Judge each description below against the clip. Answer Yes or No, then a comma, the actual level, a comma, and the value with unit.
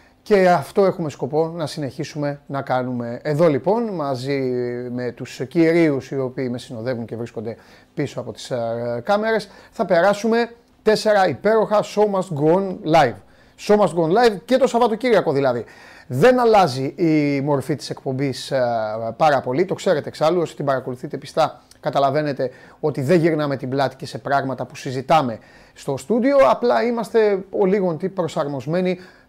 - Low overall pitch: No, medium, 155 Hz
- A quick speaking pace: No, average, 150 wpm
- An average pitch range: No, wide, 6.6 semitones